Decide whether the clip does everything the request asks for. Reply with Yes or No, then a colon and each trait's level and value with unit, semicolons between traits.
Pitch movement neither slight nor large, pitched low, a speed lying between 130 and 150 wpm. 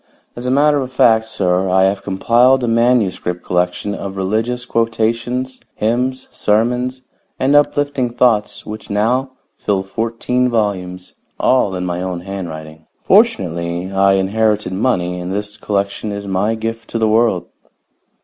Yes: average, 4.4 semitones; low, 110 Hz; average, 140 wpm